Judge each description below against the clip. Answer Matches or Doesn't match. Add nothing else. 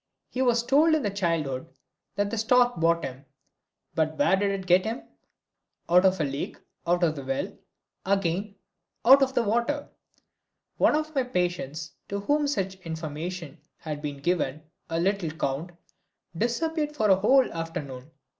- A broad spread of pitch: Matches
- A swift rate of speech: Doesn't match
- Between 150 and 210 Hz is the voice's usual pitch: Matches